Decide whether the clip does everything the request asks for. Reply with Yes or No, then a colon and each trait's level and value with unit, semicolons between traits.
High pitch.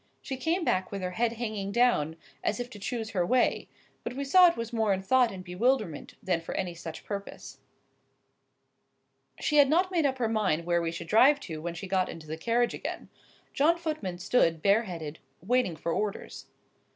Yes: high, 210 Hz